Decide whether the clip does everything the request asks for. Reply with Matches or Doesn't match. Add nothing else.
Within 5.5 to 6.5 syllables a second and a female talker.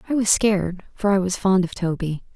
Matches